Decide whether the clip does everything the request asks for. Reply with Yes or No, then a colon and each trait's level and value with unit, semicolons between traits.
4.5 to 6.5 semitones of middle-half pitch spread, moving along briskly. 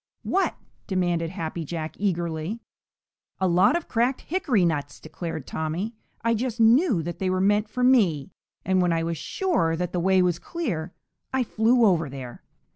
No: wide, 5.6 semitones; average, 170 wpm